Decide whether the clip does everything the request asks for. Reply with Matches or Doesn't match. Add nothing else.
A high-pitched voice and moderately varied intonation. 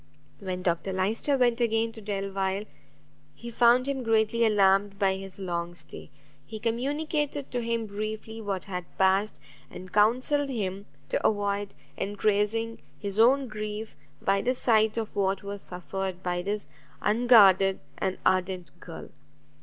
Matches